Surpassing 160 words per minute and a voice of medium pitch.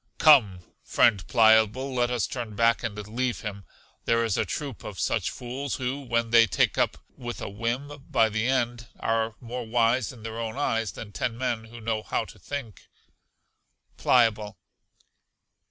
No: average, 170 wpm; low, 115 Hz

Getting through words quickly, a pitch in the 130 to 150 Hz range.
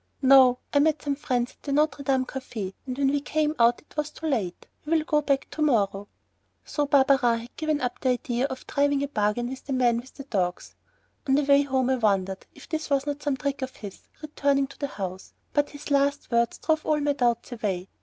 No: fast, 230 wpm; very high, 270 Hz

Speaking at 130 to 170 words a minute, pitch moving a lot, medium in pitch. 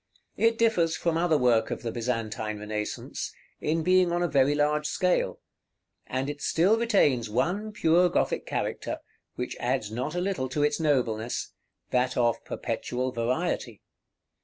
Yes: average, 150 wpm; wide, 6.2 semitones; medium, 145 Hz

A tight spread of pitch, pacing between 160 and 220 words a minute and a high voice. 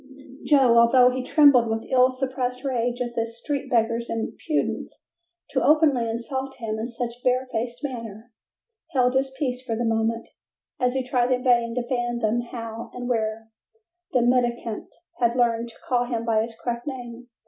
Yes: narrow, 1.7 semitones; average, 165 wpm; high, 240 Hz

